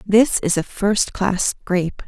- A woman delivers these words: Yes, female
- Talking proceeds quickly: No, average, 145 wpm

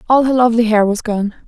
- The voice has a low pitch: No, high, 230 Hz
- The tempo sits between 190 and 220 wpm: No, fast, 245 wpm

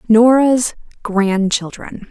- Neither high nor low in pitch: No, high, 220 Hz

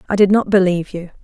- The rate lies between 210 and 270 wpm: Yes, fast, 245 wpm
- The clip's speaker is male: No, female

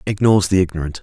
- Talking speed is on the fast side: No, average, 175 wpm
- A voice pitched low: Yes, very low, 90 Hz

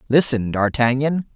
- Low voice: Yes, low, 130 Hz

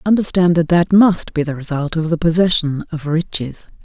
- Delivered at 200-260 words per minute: No, average, 190 wpm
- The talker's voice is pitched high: No, medium, 165 Hz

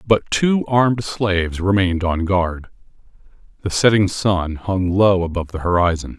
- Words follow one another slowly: No, average, 145 wpm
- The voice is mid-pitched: No, very low, 95 Hz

